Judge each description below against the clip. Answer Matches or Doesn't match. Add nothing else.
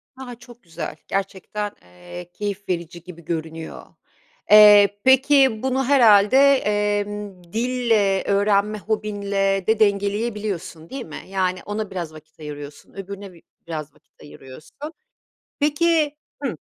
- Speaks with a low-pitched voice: Doesn't match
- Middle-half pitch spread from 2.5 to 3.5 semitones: Doesn't match